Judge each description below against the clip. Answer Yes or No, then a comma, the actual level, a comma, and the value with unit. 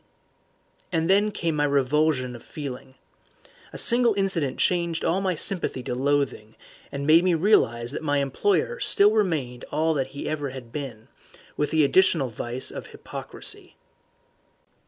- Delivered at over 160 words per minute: No, average, 150 wpm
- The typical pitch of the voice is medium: Yes, medium, 150 Hz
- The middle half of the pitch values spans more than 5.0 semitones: Yes, wide, 5.4 semitones